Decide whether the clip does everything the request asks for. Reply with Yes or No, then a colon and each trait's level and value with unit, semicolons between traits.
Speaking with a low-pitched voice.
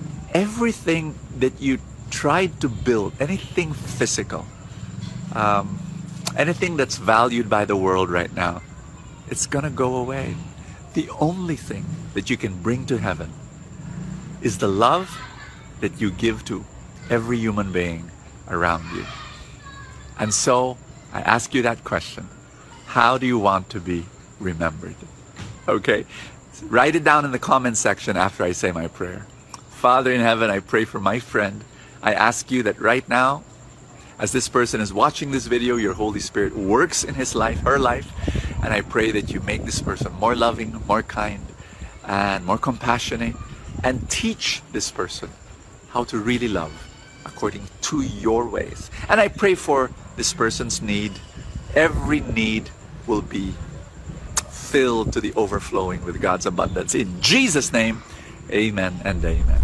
Yes: low, 120 Hz